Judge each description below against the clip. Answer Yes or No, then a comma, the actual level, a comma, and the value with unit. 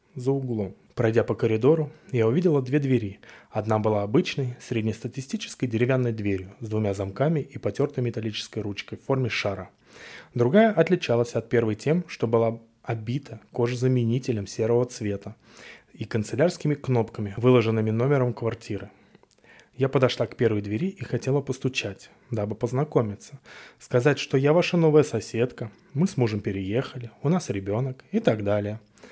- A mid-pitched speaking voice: No, low, 120 Hz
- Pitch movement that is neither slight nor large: Yes, average, 3.8 semitones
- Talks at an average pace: Yes, average, 140 wpm